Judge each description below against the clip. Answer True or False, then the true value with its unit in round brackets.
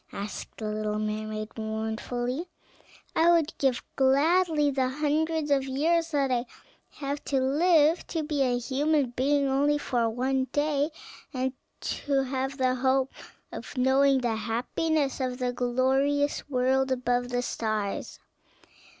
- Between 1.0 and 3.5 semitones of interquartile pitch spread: True (2.9 semitones)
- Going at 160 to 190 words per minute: False (140 wpm)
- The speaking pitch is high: True (265 Hz)